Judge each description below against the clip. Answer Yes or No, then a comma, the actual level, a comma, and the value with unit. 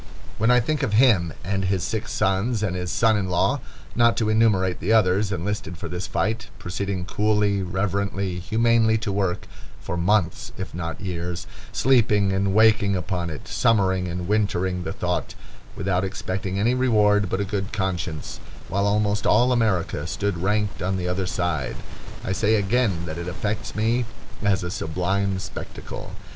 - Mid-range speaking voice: No, low, 100 Hz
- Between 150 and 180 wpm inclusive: Yes, average, 165 wpm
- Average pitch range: Yes, average, 3.0 semitones